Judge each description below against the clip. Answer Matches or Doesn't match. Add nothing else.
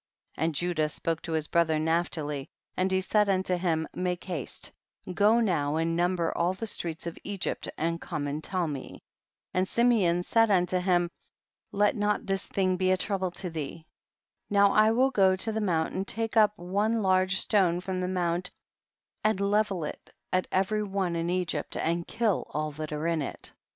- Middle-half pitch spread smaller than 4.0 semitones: Matches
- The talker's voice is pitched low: Doesn't match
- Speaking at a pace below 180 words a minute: Doesn't match